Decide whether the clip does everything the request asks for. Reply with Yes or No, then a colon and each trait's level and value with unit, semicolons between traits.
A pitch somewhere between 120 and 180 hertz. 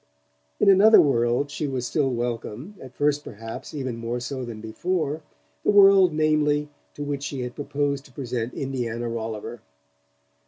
Yes: low, 135 Hz